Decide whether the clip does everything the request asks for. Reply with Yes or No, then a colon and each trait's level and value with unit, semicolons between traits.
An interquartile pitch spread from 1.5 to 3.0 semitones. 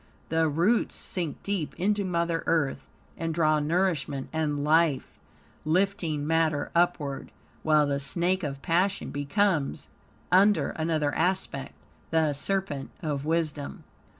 No: average, 3.4 semitones